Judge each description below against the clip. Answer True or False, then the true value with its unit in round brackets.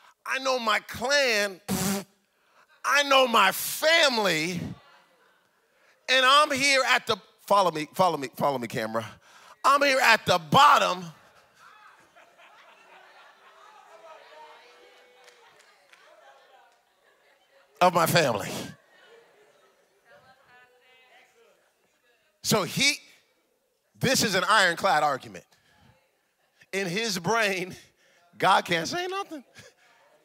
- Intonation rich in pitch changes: True (7.7 semitones)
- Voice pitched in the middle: False (220 Hz)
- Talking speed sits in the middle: False (85 wpm)